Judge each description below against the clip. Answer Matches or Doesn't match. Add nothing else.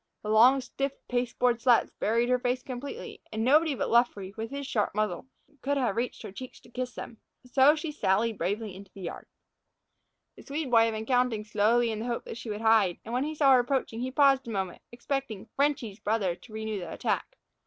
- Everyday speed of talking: Doesn't match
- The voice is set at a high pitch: Matches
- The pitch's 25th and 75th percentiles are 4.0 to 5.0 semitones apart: Doesn't match